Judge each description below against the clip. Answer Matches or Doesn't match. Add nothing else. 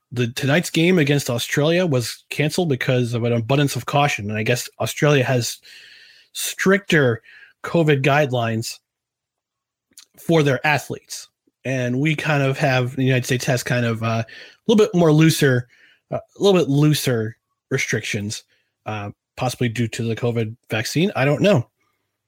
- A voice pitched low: Matches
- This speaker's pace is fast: Doesn't match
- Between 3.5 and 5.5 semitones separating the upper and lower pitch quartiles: Matches